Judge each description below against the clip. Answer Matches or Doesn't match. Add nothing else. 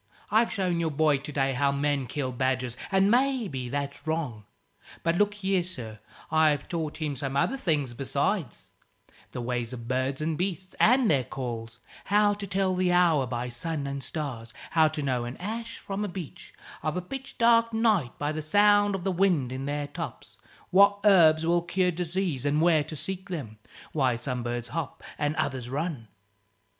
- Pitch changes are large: Matches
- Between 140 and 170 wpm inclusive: Doesn't match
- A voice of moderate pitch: Matches